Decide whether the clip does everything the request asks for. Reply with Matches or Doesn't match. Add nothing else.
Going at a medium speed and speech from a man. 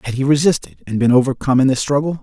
Doesn't match